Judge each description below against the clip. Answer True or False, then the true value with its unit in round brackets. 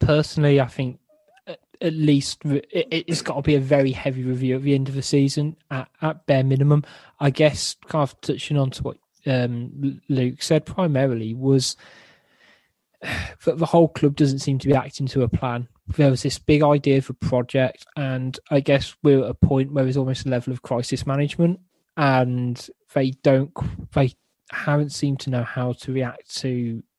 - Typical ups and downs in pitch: False (2.3 semitones)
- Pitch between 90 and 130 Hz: False (140 Hz)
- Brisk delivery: False (180 wpm)